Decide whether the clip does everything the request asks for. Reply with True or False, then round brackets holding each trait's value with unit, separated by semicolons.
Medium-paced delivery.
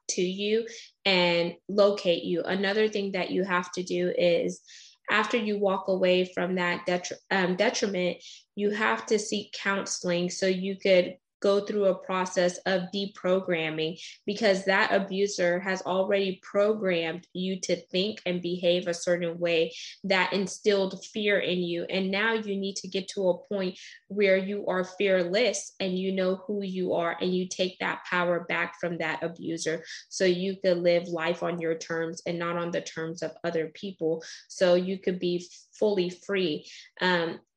True (170 wpm)